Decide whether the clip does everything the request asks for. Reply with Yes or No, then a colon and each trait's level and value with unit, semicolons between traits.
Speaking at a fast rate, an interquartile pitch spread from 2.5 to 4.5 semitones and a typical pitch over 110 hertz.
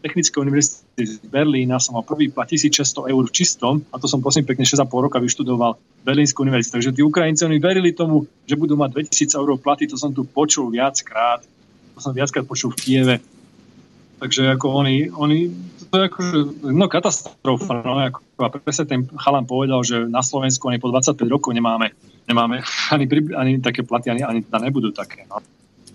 Yes: fast, 185 wpm; average, 2.8 semitones; medium, 140 Hz